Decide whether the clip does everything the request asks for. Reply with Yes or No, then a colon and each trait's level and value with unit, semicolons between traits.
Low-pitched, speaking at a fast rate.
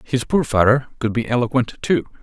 No: low, 120 Hz; average, 190 wpm